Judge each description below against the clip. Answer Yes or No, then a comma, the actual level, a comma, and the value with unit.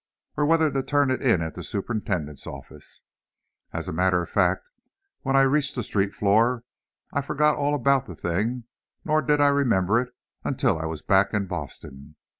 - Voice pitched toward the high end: No, low, 120 Hz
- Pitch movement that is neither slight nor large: No, wide, 7.2 semitones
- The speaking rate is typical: Yes, average, 185 wpm